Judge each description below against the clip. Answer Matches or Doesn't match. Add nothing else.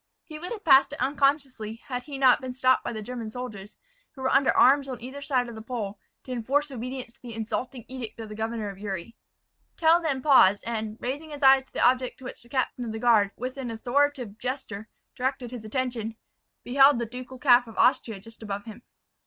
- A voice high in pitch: Matches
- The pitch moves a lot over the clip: Doesn't match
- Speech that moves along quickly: Matches